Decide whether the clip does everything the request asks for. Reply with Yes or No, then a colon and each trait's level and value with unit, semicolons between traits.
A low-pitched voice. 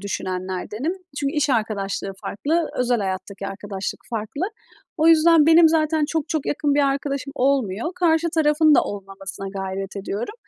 No: very high, 255 Hz